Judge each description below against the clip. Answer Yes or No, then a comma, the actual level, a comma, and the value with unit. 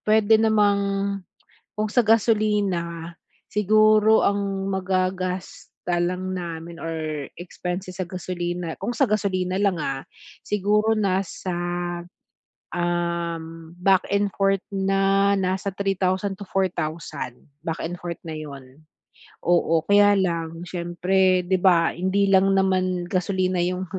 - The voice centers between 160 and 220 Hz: Yes, medium, 185 Hz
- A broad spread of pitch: No, narrow, 2.4 semitones